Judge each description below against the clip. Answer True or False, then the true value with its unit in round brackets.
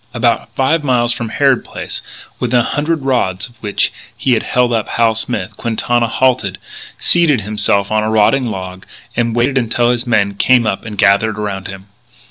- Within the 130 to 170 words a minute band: False (180 wpm)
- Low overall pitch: True (115 Hz)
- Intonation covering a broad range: False (3.2 semitones)